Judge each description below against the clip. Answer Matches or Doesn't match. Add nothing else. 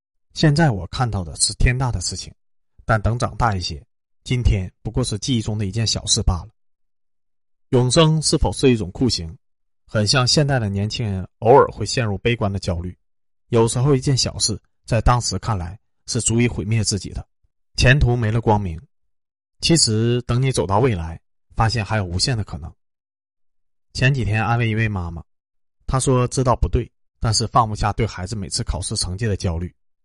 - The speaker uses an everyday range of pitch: Matches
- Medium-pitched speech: Doesn't match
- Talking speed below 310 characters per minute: Matches